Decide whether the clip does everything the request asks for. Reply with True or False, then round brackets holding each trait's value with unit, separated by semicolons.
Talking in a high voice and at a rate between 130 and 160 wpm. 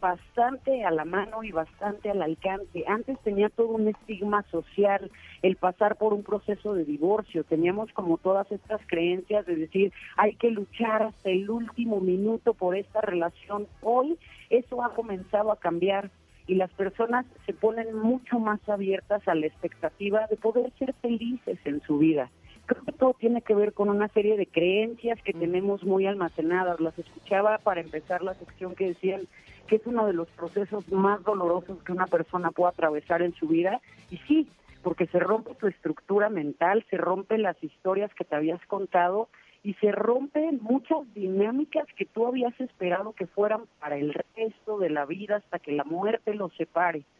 False (200 Hz; 180 wpm)